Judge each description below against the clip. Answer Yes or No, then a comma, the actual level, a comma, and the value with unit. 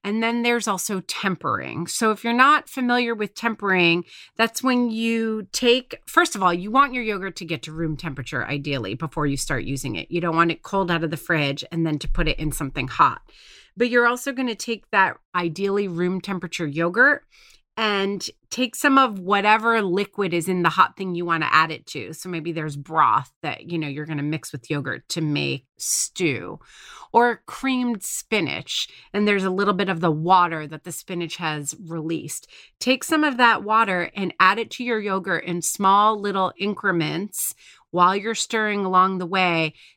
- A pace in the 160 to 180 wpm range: No, average, 195 wpm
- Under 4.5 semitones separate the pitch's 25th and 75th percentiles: No, average, 5.3 semitones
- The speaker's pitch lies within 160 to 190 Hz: Yes, medium, 185 Hz